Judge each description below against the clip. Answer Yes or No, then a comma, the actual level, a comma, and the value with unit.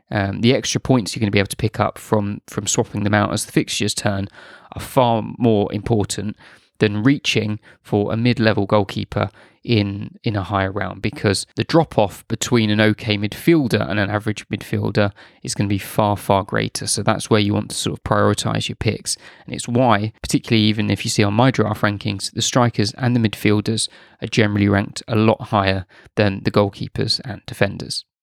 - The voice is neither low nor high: No, low, 105 Hz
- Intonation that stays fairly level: Yes, narrow, 2.1 semitones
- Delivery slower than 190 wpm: No, average, 200 wpm